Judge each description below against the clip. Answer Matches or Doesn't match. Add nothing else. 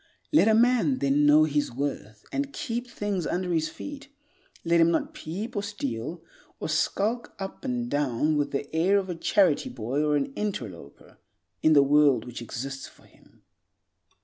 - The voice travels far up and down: Matches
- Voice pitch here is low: Doesn't match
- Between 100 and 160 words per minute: Doesn't match